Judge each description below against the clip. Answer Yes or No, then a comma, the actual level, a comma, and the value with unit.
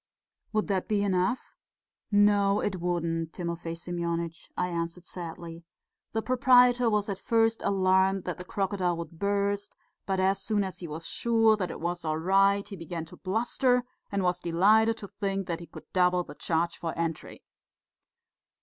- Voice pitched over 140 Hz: Yes, medium, 185 Hz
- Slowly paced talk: No, average, 170 wpm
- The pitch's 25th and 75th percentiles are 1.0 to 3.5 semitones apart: Yes, average, 3.2 semitones